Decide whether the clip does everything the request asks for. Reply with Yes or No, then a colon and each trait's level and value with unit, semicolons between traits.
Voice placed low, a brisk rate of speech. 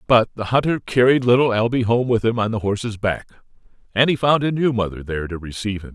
Yes: low, 115 Hz; fast, 230 wpm